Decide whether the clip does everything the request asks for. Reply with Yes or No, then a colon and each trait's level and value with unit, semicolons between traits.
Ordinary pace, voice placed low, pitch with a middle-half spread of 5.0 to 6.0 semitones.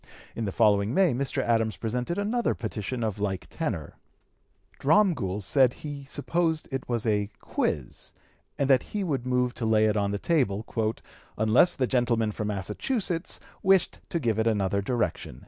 Yes: average, 165 wpm; low, 120 Hz; wide, 5.5 semitones